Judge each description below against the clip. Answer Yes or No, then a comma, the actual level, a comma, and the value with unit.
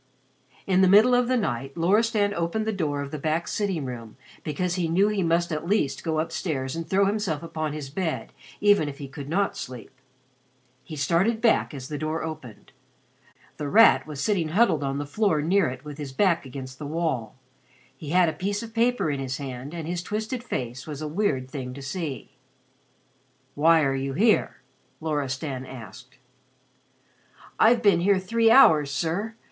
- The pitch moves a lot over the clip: Yes, wide, 6.0 semitones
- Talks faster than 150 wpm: Yes, average, 185 wpm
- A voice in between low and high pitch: Yes, medium, 160 Hz